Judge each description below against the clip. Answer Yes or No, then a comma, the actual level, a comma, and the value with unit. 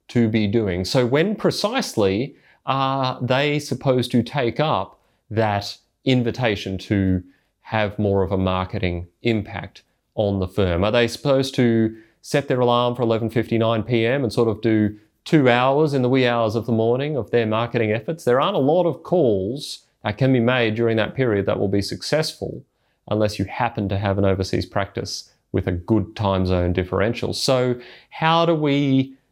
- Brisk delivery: No, average, 175 wpm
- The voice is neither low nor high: No, low, 115 Hz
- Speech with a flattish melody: No, average, 4.5 semitones